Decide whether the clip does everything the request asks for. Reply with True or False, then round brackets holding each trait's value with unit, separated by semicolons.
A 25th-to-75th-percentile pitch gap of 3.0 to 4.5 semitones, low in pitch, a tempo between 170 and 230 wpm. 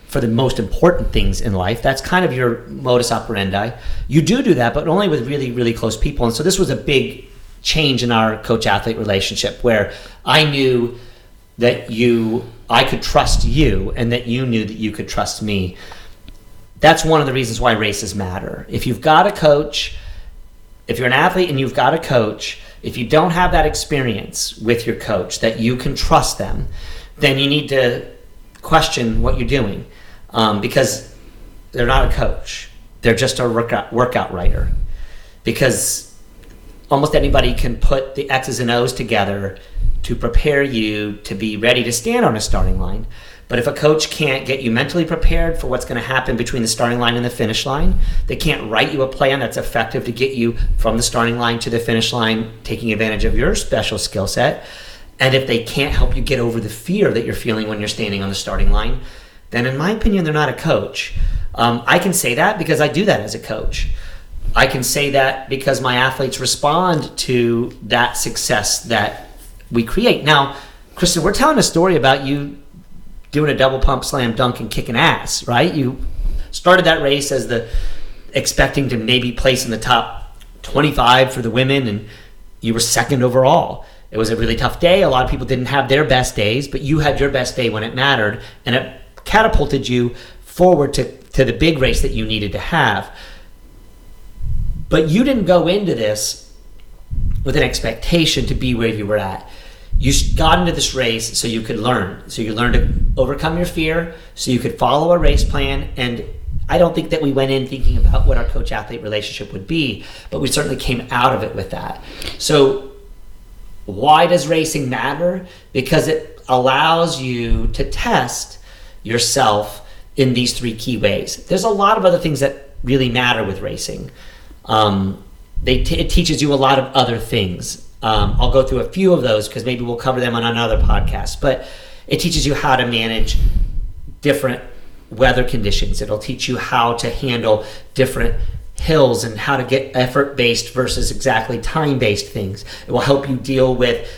True (4.1 semitones; 125 Hz; 195 wpm)